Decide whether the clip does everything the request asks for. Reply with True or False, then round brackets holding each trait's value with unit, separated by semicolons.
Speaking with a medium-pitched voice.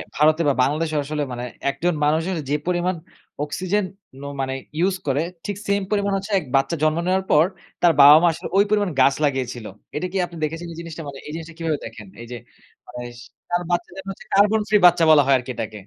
True (165 Hz)